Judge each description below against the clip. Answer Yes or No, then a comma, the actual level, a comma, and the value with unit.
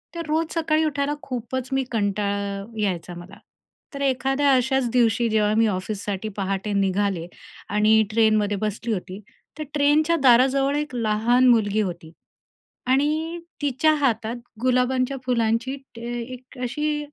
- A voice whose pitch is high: Yes, high, 240 Hz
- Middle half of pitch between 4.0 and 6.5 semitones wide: Yes, average, 4.7 semitones